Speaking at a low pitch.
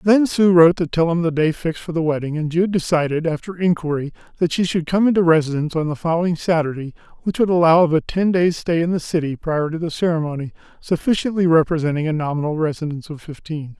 No: medium, 165 Hz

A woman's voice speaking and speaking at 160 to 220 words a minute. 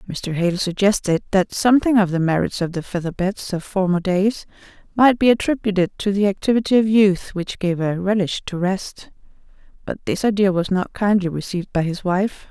Yes: female; average, 180 wpm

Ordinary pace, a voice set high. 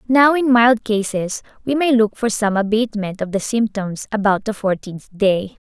Yes: average, 180 wpm; high, 215 Hz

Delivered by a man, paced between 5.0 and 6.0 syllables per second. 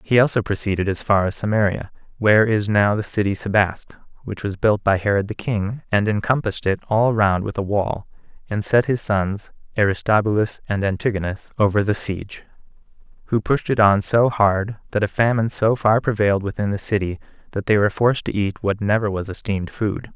Yes: male; 5.7 syllables/s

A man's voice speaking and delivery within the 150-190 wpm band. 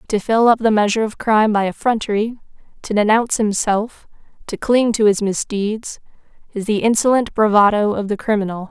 No: female; average, 165 wpm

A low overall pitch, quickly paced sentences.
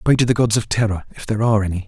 Yes: low, 110 Hz; fast, 320 wpm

